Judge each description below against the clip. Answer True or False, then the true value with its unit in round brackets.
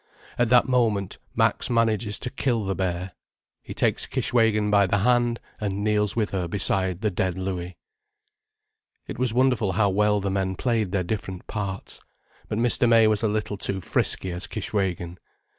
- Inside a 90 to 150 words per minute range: False (165 wpm)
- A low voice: True (105 Hz)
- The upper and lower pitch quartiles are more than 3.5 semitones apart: False (3.1 semitones)